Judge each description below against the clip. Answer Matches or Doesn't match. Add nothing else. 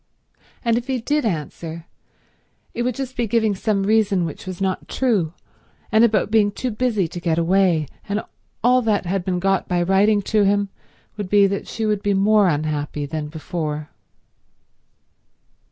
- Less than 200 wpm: Matches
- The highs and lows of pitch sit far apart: Doesn't match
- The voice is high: Matches